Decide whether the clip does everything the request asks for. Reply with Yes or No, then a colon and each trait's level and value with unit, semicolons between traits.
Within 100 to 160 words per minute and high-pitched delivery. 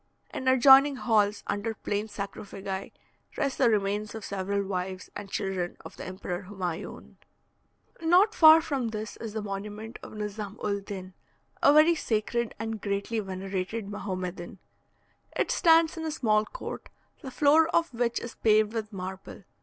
Yes: average, 155 wpm; high, 215 Hz